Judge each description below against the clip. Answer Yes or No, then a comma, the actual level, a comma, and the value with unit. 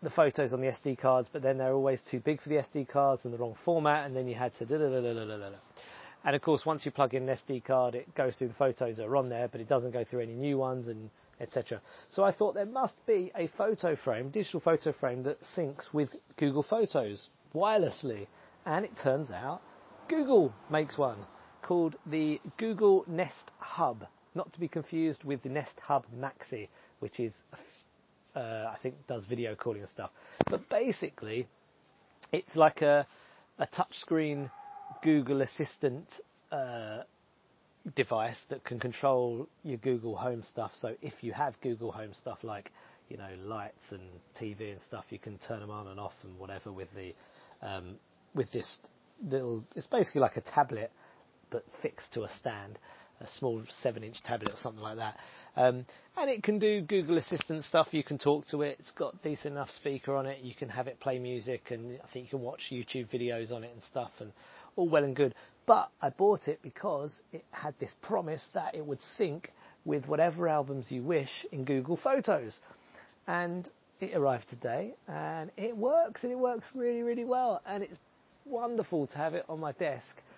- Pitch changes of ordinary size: Yes, average, 5.0 semitones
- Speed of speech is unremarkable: Yes, average, 190 wpm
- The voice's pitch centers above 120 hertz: Yes, medium, 140 Hz